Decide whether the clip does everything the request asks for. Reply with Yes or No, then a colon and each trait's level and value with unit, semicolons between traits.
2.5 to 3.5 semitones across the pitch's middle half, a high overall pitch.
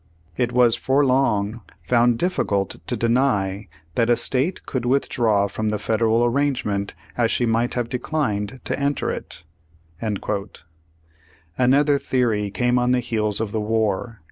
No: average, 3.1 semitones; low, 120 Hz